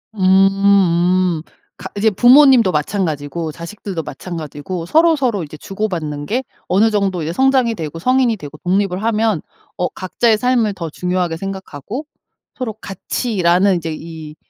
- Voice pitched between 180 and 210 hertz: Yes, high, 190 Hz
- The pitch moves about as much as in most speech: Yes, average, 4.7 semitones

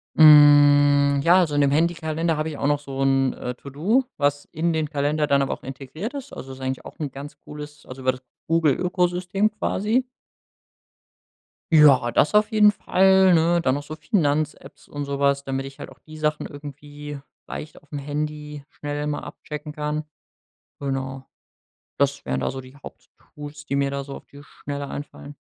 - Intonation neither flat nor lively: No, narrow, 2.1 semitones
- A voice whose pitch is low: No, medium, 145 Hz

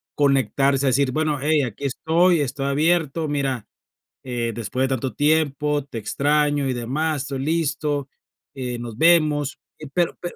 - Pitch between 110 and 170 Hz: Yes, medium, 140 Hz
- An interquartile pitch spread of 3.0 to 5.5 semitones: No, narrow, 2.6 semitones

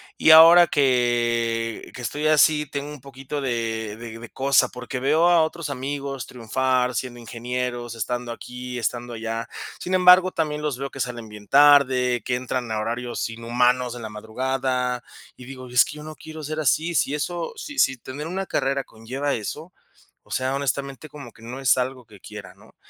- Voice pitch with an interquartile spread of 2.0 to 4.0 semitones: Yes, average, 3.3 semitones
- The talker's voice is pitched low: Yes, low, 130 Hz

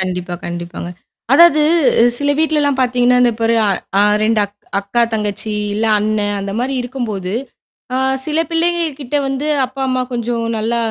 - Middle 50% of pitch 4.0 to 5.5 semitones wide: Yes, average, 4.7 semitones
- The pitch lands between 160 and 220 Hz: No, high, 240 Hz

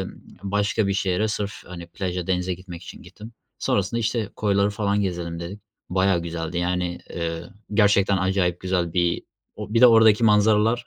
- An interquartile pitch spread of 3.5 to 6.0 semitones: No, average, 2.9 semitones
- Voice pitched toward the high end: No, very low, 95 Hz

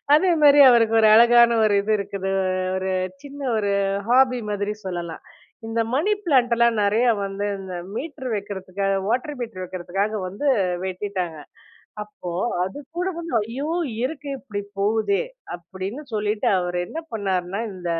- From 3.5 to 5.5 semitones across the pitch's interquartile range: Yes, average, 4.6 semitones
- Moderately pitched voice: No, high, 210 Hz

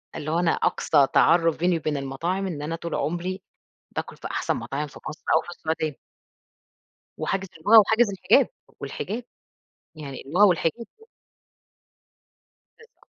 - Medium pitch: Yes, medium, 165 Hz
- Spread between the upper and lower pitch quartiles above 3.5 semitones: Yes, average, 3.9 semitones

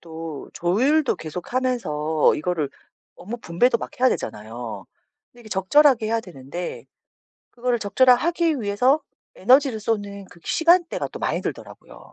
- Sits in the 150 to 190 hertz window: No, high, 215 Hz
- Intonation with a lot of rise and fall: Yes, wide, 7.3 semitones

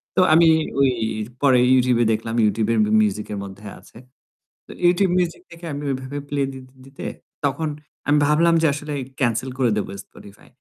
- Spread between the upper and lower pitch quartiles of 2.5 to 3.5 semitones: No, average, 5.0 semitones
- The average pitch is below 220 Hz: Yes, low, 135 Hz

